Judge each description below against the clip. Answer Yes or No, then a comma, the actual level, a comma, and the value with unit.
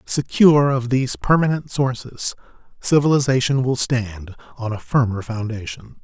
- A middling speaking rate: No, slow, 120 wpm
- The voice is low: Yes, low, 125 Hz